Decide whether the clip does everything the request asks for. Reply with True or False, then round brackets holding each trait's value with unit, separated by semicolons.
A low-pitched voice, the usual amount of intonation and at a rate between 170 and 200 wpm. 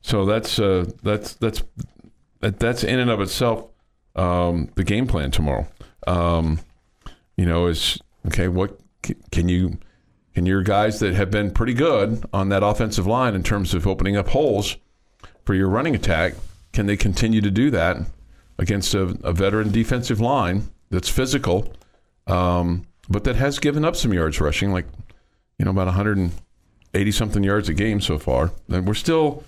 True (100 Hz; 3.5 semitones; 175 wpm)